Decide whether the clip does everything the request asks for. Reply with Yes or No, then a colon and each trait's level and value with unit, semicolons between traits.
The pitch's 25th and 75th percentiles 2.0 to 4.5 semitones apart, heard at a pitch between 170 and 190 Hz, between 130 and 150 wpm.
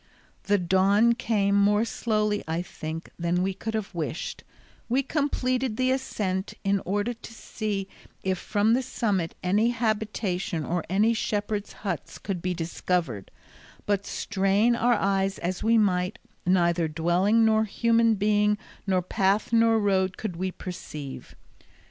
No: average, 3.3 semitones; high, 200 Hz; average, 140 wpm